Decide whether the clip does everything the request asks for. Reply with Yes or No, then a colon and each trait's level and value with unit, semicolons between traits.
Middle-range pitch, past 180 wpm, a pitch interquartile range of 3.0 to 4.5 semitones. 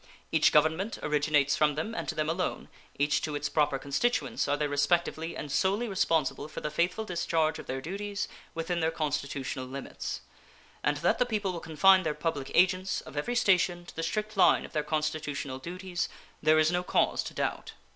Yes: medium, 160 Hz; average, 190 wpm; average, 3.7 semitones